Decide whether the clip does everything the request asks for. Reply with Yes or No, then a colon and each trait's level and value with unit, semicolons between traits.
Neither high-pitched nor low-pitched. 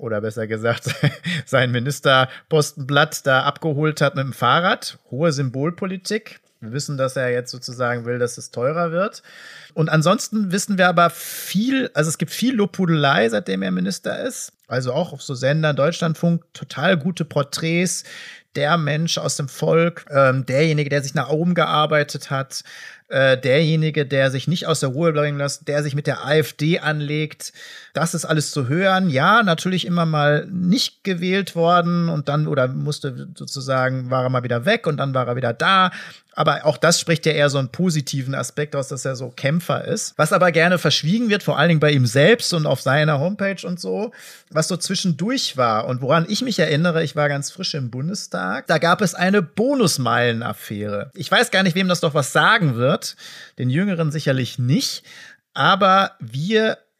Yes: medium, 155 Hz